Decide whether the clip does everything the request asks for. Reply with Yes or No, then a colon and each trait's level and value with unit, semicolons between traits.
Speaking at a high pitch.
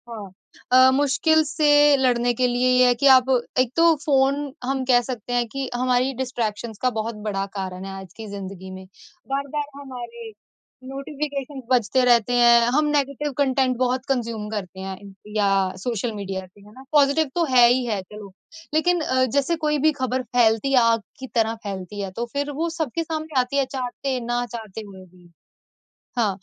Yes: high, 245 Hz